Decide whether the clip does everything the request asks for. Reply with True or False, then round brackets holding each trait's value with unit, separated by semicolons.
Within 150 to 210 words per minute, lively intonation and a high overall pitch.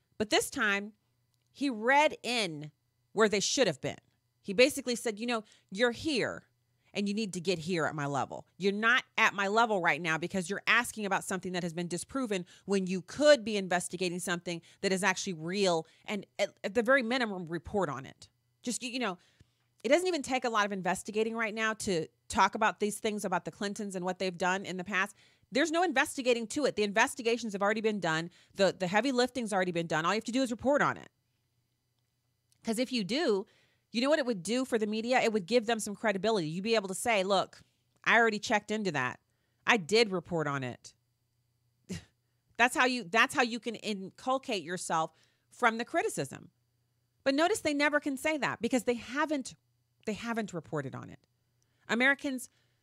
True (205 wpm; 6.3 semitones; 200 Hz)